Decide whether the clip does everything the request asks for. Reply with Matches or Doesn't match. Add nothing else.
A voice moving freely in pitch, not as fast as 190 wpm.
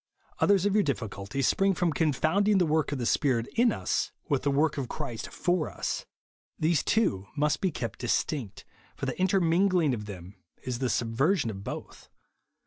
Matches